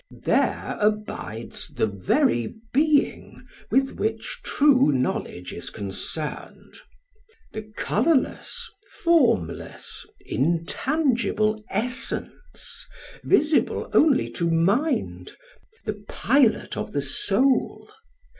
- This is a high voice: Yes, high, 215 Hz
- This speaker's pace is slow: Yes, slow, 80 wpm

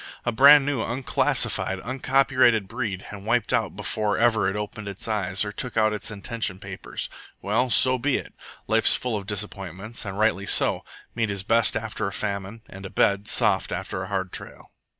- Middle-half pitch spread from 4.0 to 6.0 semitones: No, average, 3.0 semitones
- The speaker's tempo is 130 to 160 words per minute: No, average, 185 wpm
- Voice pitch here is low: Yes, low, 105 Hz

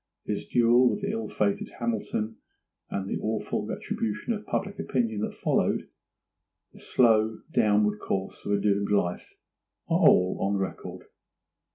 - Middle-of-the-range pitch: No, low, 110 Hz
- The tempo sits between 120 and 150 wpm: Yes, average, 140 wpm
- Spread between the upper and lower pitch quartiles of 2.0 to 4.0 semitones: Yes, average, 2.8 semitones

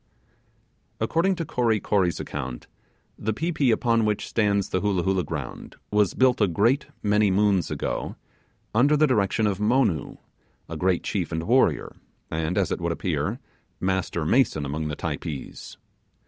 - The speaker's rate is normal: Yes, average, 155 wpm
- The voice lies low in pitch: Yes, low, 100 Hz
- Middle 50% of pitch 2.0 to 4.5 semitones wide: No, average, 5.3 semitones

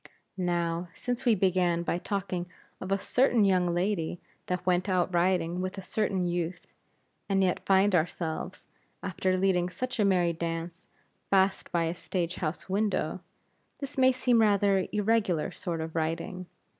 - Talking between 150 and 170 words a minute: Yes, average, 155 wpm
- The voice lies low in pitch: No, medium, 185 Hz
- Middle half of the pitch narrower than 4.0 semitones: Yes, narrow, 2.4 semitones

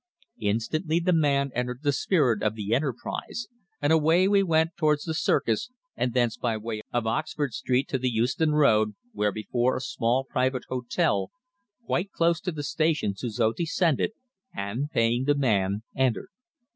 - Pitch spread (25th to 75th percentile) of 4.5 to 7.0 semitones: Yes, wide, 5.5 semitones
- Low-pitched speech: Yes, low, 130 Hz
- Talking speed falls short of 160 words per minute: No, average, 165 wpm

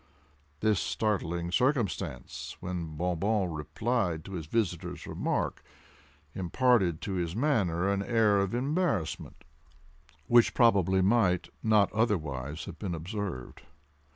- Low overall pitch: Yes, very low, 95 Hz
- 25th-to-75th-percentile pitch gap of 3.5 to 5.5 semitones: Yes, average, 4.6 semitones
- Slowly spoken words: Yes, slow, 115 wpm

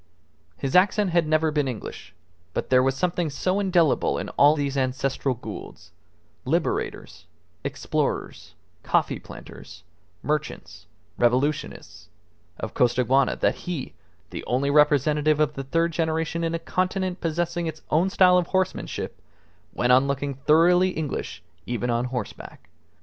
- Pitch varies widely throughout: No, average, 4.4 semitones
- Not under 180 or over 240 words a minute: No, slow, 135 wpm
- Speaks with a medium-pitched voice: Yes, medium, 150 Hz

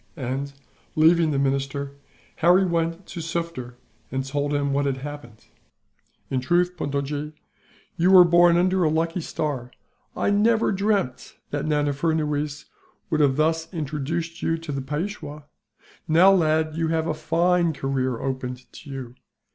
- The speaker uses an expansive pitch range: No, average, 3.4 semitones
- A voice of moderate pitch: Yes, medium, 155 Hz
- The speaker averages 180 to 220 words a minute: No, average, 145 wpm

